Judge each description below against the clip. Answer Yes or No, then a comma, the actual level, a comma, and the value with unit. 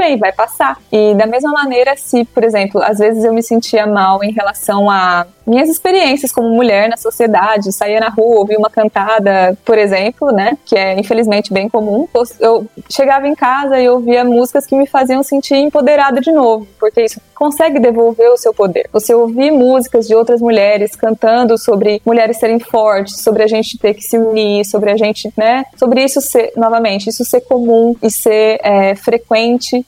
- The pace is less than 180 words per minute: No, fast, 185 wpm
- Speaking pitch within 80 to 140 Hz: No, high, 230 Hz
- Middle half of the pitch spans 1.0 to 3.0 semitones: Yes, average, 2.7 semitones